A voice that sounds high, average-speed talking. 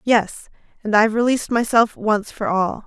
Yes: high, 220 Hz; average, 165 wpm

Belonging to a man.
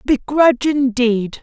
No: female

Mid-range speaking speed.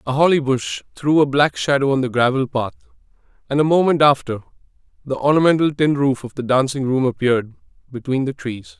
Yes: average, 185 wpm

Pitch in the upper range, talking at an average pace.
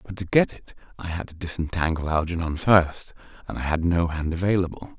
No: very low, 85 Hz; average, 195 wpm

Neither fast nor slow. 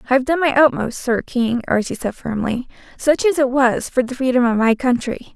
No: fast, 225 wpm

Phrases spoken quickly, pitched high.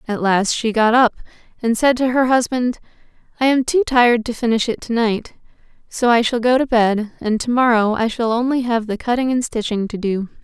Yes: fast, 220 wpm; high, 235 Hz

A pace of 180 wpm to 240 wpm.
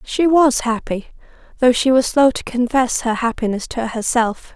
No: average, 170 wpm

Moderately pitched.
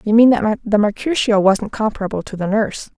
No: high, 215 Hz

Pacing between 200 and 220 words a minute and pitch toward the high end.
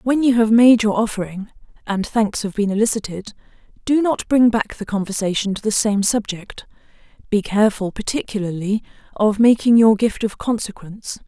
No: average, 160 wpm; high, 215 Hz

